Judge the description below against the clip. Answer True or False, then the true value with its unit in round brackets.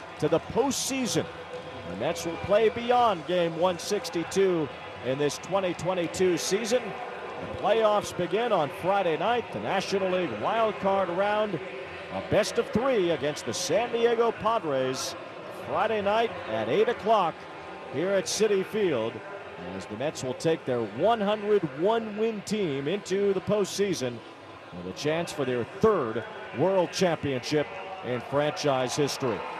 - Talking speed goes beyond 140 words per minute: False (135 wpm)